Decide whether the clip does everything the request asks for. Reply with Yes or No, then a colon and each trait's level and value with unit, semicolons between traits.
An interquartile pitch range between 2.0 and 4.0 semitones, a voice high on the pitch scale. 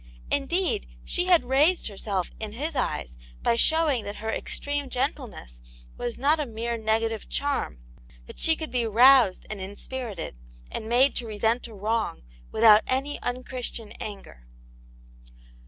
No: average, 4.5 semitones; high, 235 Hz